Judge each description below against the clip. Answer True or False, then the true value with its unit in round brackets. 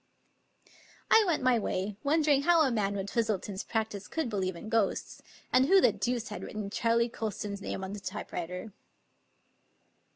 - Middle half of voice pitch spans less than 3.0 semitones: False (4.1 semitones)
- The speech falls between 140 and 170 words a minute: True (160 wpm)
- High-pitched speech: True (220 Hz)